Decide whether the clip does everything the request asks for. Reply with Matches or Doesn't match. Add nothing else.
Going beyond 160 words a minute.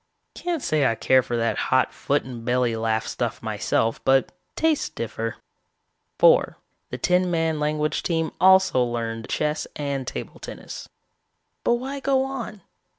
Doesn't match